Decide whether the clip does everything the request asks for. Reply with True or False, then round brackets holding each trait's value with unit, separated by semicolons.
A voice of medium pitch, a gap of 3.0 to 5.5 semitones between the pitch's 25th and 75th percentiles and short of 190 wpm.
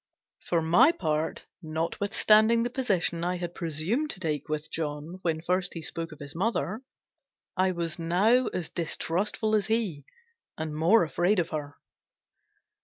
True (170 Hz; 4.5 semitones; 150 wpm)